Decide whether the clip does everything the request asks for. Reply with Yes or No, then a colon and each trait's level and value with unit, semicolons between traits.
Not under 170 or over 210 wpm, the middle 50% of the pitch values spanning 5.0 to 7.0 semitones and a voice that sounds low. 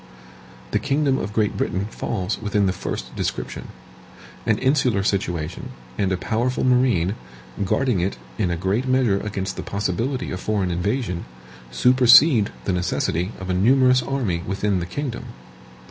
No: average, 145 wpm; wide, 5.4 semitones; low, 105 Hz